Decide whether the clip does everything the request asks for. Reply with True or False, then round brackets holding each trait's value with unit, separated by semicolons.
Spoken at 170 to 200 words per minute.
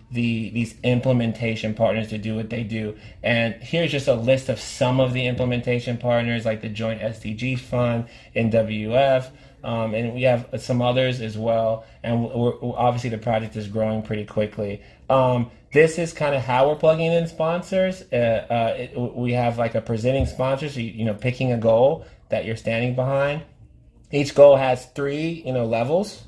True (185 wpm)